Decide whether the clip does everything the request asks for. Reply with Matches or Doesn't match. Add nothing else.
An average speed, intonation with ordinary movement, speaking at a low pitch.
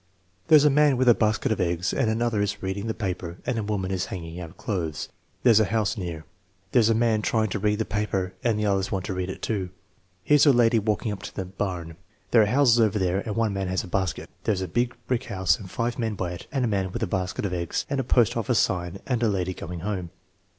Doesn't match